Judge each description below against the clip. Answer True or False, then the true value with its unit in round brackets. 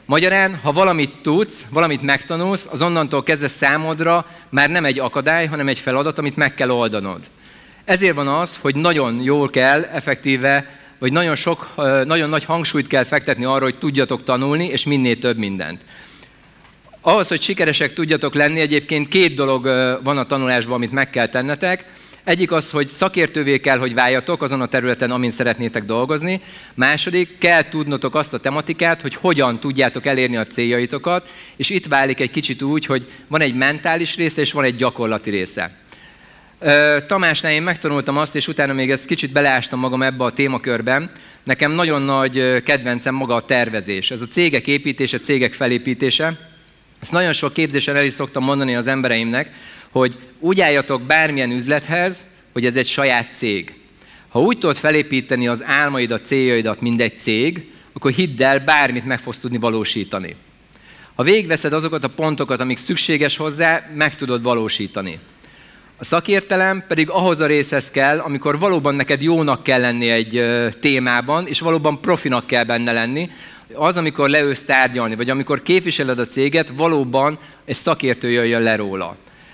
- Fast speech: True (160 wpm)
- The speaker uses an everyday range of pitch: True (3.7 semitones)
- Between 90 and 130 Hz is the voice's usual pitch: False (140 Hz)